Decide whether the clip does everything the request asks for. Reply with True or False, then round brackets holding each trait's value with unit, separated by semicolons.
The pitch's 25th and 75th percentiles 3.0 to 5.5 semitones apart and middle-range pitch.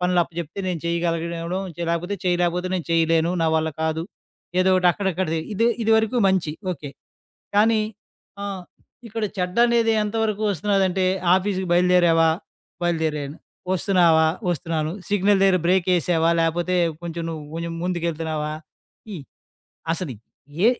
False (2.5 semitones; 175 Hz)